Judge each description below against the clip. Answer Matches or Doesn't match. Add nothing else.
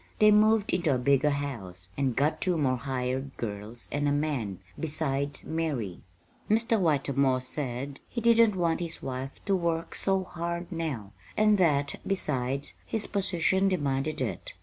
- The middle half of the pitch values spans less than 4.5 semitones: Doesn't match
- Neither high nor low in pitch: Matches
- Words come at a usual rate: Matches